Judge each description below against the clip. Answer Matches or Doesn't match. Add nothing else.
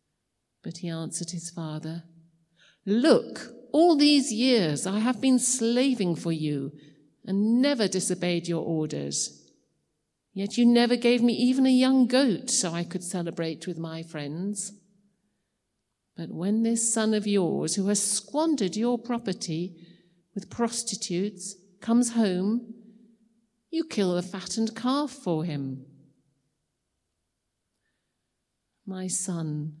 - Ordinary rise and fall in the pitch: Doesn't match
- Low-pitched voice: Doesn't match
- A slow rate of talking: Matches